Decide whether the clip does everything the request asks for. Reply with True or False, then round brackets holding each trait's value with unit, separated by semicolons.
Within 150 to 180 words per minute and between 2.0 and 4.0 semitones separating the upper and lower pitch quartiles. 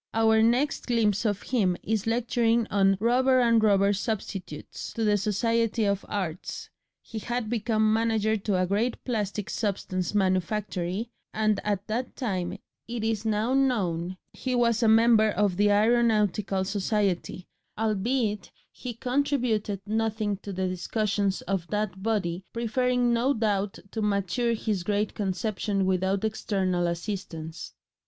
False (135 wpm; 2.9 semitones)